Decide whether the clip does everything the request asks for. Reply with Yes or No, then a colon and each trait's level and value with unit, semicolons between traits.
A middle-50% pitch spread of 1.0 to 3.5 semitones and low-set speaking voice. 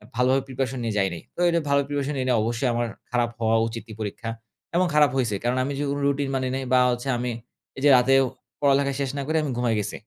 Yes: average, 2.9 semitones; low, 130 Hz